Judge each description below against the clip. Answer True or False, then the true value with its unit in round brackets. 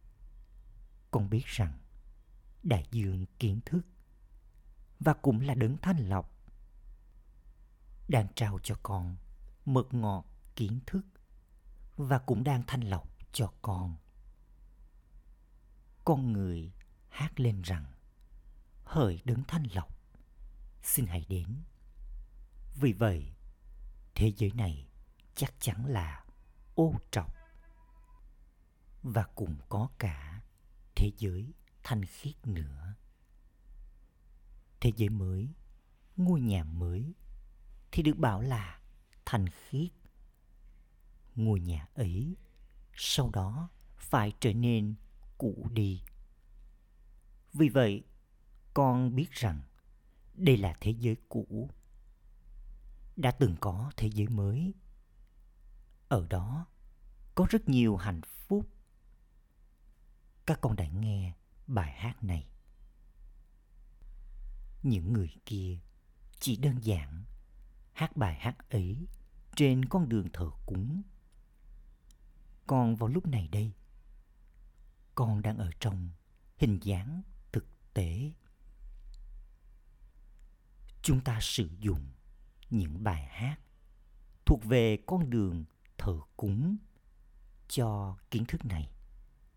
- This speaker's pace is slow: True (105 wpm)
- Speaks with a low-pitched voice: True (105 Hz)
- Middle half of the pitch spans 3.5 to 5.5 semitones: True (5.2 semitones)